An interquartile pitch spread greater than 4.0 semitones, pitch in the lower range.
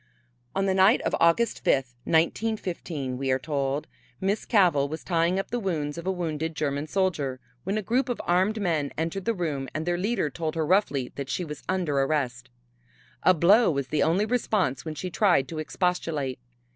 No: average, 4.9 semitones; medium, 165 Hz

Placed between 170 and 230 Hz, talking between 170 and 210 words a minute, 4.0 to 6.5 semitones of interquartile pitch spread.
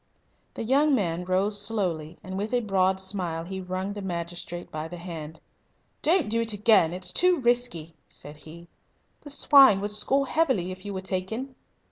Yes: high, 190 Hz; average, 175 wpm; average, 4.8 semitones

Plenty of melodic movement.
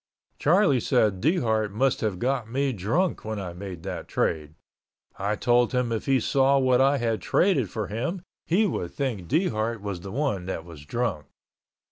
Yes: wide, 5.7 semitones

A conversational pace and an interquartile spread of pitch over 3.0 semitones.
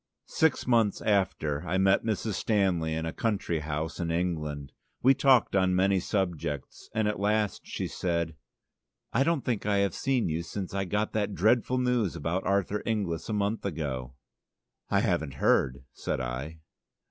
Yes: average, 165 wpm; average, 4.9 semitones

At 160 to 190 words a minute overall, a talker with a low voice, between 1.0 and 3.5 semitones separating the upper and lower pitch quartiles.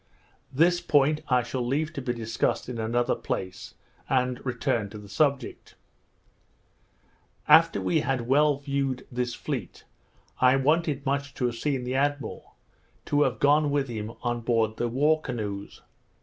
No: average, 150 wpm; low, 130 Hz; average, 3.2 semitones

